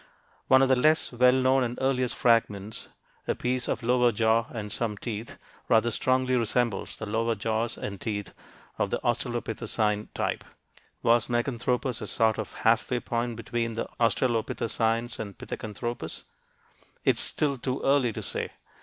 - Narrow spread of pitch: Yes, narrow, 2.0 semitones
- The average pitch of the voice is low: Yes, low, 120 Hz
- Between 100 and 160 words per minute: Yes, average, 155 wpm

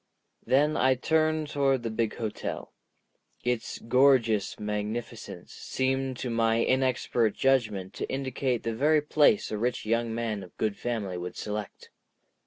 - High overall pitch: No, low, 120 Hz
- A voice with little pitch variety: No, average, 3.4 semitones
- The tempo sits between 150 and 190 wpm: No, average, 140 wpm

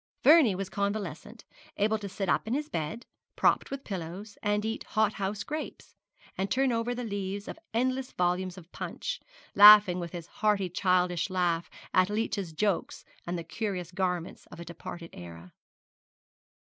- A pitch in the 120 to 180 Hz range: No, high, 195 Hz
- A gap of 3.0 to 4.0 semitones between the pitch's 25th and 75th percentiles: Yes, average, 3.5 semitones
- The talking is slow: No, average, 160 wpm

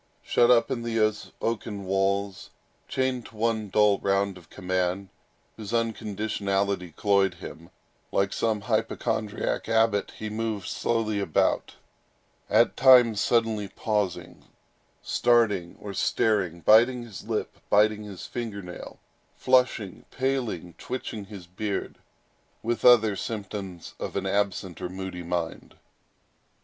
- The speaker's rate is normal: No, slow, 120 wpm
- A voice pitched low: Yes, low, 105 Hz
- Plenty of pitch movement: No, average, 2.8 semitones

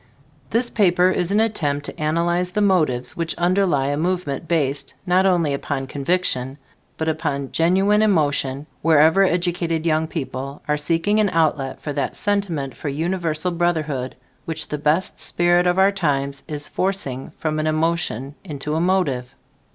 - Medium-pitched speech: Yes, medium, 160 Hz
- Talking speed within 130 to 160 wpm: Yes, average, 155 wpm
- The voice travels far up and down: No, average, 4.0 semitones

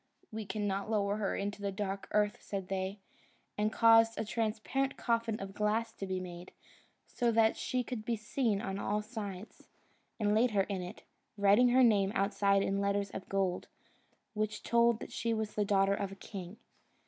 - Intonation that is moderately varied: No, narrow, 2.2 semitones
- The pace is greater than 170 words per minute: Yes, average, 185 wpm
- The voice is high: Yes, high, 210 Hz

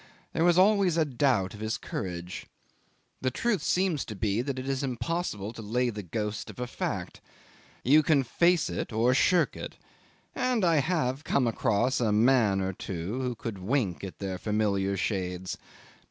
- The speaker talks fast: No, average, 175 wpm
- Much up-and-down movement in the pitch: Yes, wide, 6.4 semitones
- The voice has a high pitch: No, low, 120 Hz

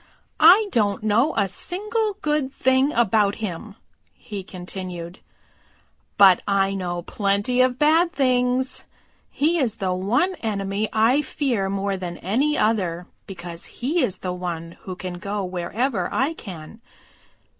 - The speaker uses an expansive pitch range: Yes, wide, 5.9 semitones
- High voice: Yes, high, 205 Hz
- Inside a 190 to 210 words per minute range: No, slow, 135 wpm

